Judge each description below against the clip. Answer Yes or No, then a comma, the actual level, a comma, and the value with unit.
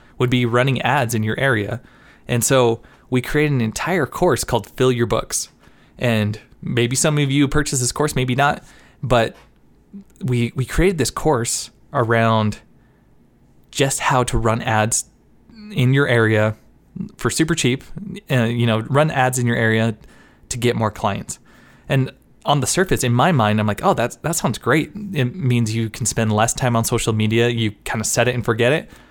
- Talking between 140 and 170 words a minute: No, average, 185 wpm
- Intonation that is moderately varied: Yes, average, 3.3 semitones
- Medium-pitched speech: No, low, 120 Hz